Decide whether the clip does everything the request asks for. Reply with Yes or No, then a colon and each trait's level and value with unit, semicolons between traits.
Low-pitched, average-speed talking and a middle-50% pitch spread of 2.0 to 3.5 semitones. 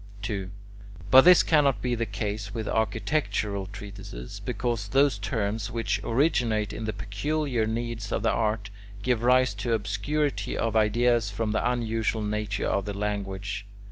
Yes: low, 110 Hz; average, 150 wpm; average, 2.9 semitones